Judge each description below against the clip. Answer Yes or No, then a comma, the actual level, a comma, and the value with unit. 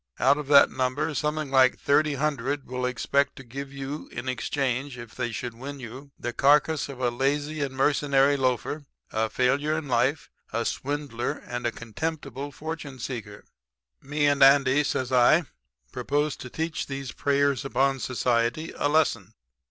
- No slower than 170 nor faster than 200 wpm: No, average, 160 wpm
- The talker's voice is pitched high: No, low, 135 Hz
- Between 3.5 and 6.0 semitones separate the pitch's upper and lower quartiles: No, narrow, 2.4 semitones